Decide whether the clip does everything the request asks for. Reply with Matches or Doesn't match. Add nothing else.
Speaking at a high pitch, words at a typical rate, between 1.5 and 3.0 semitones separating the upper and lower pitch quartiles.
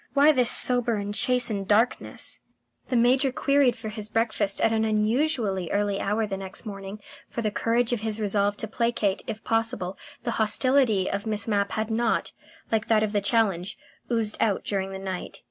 Matches